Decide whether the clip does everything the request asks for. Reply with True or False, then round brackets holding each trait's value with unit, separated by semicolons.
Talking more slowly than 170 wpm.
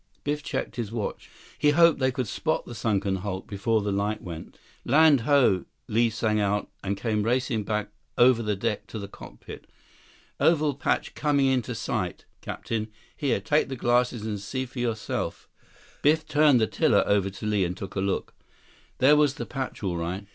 False (185 wpm)